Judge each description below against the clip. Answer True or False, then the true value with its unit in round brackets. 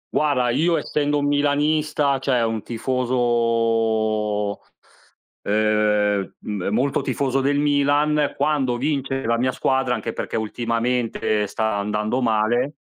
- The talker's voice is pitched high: False (125 Hz)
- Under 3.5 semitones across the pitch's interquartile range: False (4.5 semitones)